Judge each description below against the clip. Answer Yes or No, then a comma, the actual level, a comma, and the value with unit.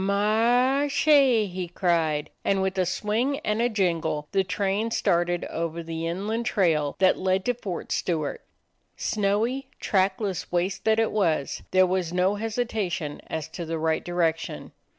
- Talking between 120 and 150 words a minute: No, average, 165 wpm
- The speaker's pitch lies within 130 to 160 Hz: No, high, 190 Hz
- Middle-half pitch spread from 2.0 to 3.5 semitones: No, average, 4.3 semitones